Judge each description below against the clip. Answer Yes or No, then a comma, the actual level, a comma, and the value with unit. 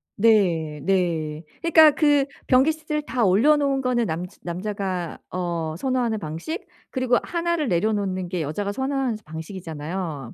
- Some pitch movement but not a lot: No, wide, 7.9 semitones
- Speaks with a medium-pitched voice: No, high, 200 Hz